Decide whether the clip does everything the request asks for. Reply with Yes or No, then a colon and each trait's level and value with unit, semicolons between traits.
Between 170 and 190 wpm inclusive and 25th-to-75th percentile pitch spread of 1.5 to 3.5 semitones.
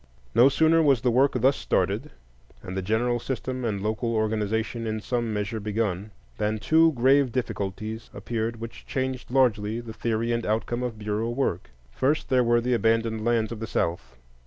Yes: average, 175 wpm; narrow, 2.4 semitones